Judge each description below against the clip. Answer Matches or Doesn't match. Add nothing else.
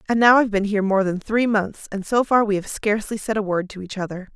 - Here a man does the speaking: Doesn't match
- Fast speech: Matches